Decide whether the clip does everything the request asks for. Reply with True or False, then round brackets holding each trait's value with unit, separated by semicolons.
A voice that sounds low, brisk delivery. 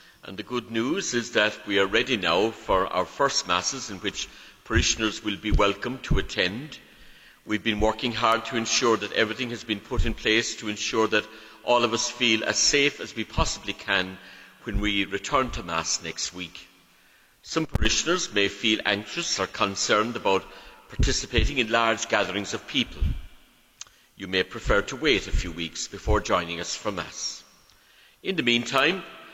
False (110 Hz; 175 wpm)